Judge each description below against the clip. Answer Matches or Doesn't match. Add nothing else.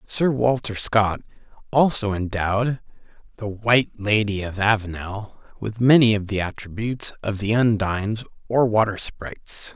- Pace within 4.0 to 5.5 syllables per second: Matches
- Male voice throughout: Matches